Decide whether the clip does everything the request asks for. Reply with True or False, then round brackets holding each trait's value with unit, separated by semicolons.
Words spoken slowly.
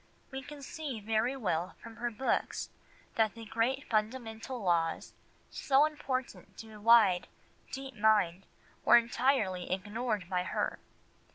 True (130 wpm)